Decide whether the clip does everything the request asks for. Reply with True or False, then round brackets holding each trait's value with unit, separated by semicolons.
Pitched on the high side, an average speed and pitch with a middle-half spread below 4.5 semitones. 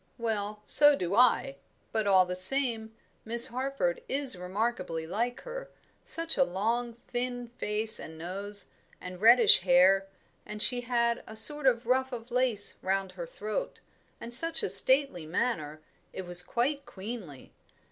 False (225 Hz; 150 wpm; 4.8 semitones)